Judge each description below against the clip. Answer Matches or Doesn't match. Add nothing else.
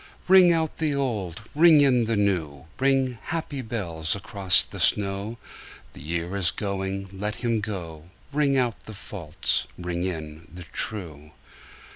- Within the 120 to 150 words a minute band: Matches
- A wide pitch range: Matches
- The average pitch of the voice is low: Matches